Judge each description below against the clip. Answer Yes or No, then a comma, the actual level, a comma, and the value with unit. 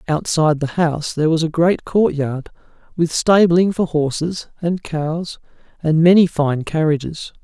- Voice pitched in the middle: Yes, medium, 160 Hz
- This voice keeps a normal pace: Yes, average, 145 wpm